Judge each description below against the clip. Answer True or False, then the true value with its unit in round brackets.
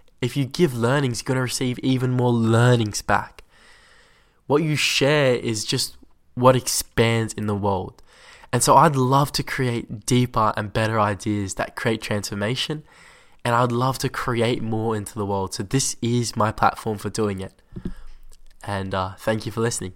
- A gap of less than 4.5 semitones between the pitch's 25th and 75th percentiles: True (3.5 semitones)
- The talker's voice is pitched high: False (115 Hz)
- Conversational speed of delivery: True (175 wpm)